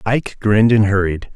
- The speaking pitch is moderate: No, low, 105 Hz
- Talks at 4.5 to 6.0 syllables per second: Yes, 5.9 syllables/s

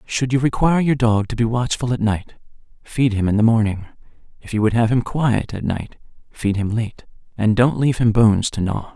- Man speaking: Yes, male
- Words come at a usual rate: No, fast, 220 wpm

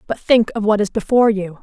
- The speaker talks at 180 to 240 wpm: No, fast, 260 wpm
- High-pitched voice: Yes, high, 210 Hz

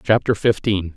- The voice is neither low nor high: No, low, 100 Hz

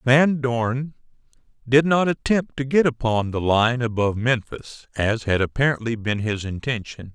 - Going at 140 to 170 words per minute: Yes, average, 150 wpm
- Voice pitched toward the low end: Yes, low, 125 Hz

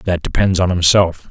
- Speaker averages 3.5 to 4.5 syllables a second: No, 4.7 syllables/s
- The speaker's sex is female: No, male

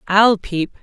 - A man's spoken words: No, female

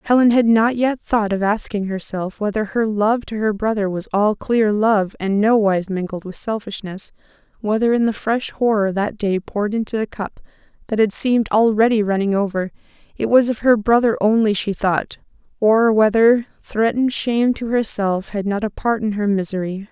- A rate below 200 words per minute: Yes, average, 180 wpm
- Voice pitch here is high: Yes, high, 215 Hz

